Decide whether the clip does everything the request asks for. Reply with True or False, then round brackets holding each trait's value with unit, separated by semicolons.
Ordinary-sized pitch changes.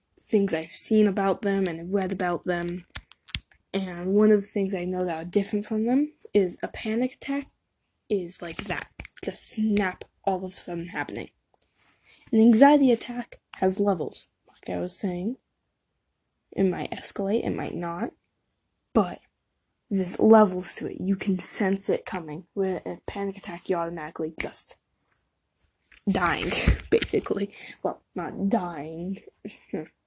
True (3.3 semitones)